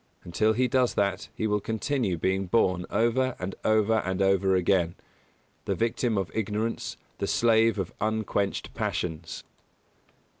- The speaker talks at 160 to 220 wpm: No, average, 140 wpm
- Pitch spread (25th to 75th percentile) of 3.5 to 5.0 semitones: No, average, 3.1 semitones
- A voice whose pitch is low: Yes, low, 105 Hz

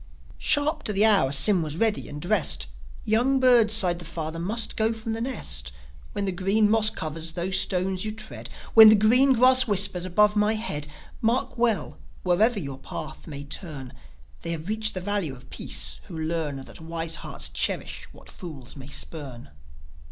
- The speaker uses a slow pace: No, average, 180 wpm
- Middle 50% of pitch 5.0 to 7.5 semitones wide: Yes, wide, 5.5 semitones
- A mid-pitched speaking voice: No, high, 195 Hz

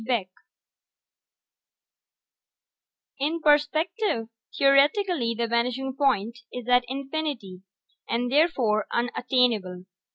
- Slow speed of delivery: Yes, slow, 75 wpm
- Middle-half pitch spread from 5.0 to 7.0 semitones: No, average, 4.0 semitones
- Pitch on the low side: No, very high, 250 Hz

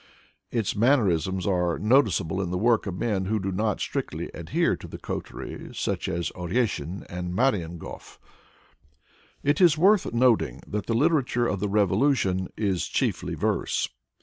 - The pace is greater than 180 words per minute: No, average, 150 wpm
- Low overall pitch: Yes, low, 100 Hz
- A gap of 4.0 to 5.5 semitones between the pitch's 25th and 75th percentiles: Yes, average, 4.8 semitones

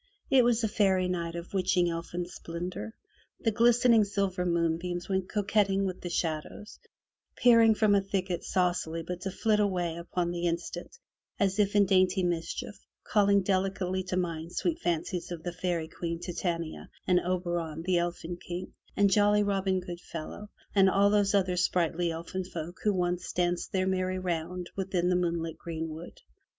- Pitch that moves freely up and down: No, narrow, 2.4 semitones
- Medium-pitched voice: Yes, medium, 180 Hz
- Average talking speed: Yes, average, 160 wpm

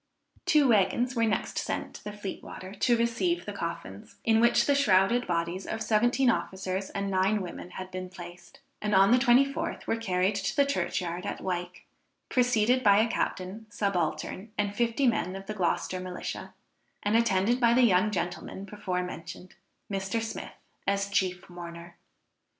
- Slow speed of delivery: No, average, 170 wpm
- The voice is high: Yes, high, 200 Hz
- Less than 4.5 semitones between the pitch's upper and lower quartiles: Yes, average, 3.8 semitones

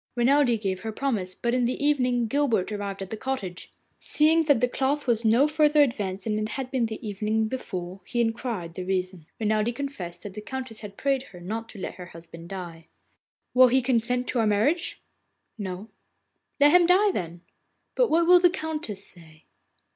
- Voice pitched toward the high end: Yes, high, 225 Hz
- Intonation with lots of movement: Yes, wide, 5.7 semitones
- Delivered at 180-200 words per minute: Yes, average, 185 wpm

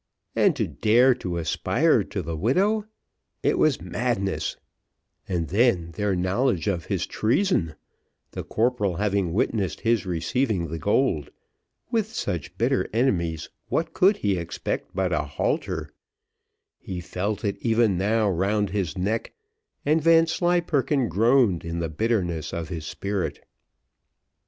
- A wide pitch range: Yes, wide, 6.2 semitones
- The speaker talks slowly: Yes, slow, 130 wpm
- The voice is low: Yes, low, 100 Hz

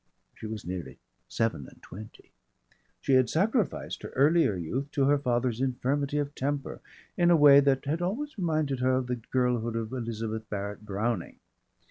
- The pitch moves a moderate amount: Yes, average, 4.5 semitones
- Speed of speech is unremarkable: Yes, average, 165 wpm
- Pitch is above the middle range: No, low, 130 Hz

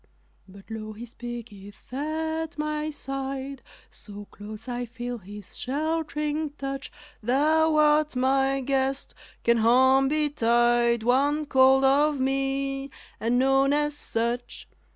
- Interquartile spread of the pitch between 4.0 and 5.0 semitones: No, average, 3.6 semitones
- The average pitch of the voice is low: No, very high, 270 Hz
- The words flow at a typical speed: No, slow, 115 wpm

